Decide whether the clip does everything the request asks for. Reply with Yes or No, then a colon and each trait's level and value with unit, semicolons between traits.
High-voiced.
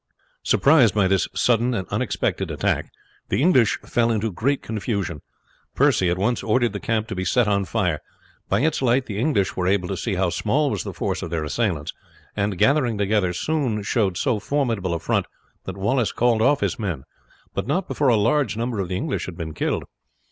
No: low, 110 Hz